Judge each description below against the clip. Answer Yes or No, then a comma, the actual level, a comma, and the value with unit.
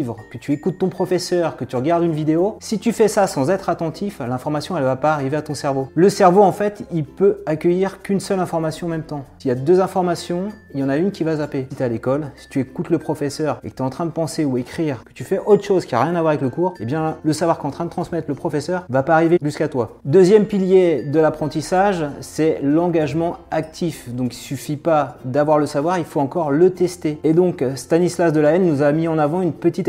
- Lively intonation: No, average, 3.8 semitones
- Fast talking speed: Yes, fast, 265 wpm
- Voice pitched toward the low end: No, medium, 160 Hz